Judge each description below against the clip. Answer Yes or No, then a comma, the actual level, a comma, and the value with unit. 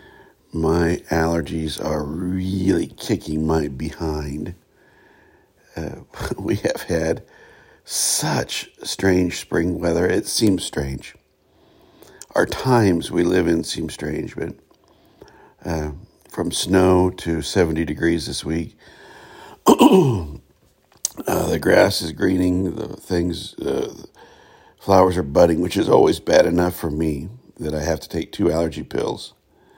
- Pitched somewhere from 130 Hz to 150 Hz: No, very low, 85 Hz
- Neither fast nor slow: No, slow, 120 wpm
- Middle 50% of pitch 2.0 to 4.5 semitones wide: Yes, average, 2.7 semitones